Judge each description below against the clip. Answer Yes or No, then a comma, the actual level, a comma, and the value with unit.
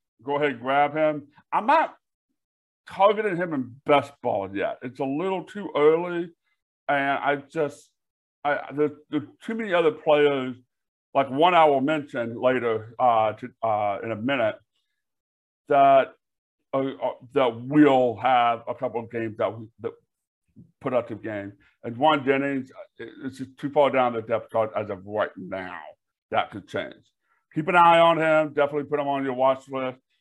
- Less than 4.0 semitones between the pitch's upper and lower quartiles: Yes, average, 3.6 semitones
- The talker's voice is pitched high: No, medium, 140 Hz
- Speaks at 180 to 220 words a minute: No, average, 165 wpm